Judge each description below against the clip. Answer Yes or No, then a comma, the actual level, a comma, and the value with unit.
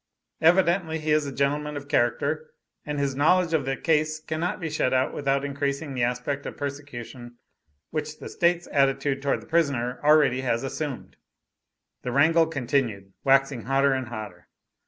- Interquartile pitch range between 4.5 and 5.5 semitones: No, average, 2.8 semitones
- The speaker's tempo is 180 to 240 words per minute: No, average, 160 wpm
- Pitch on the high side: No, medium, 140 Hz